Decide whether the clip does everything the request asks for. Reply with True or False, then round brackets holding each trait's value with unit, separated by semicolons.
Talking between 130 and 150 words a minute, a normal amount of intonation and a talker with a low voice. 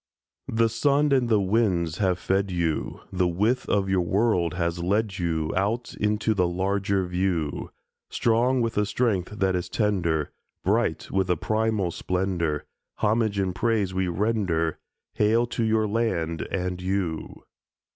True (145 wpm; 3.8 semitones; 95 Hz)